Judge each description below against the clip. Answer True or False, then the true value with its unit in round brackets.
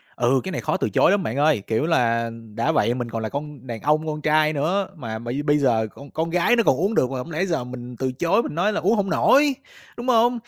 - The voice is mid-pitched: True (150 Hz)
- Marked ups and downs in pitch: True (6.6 semitones)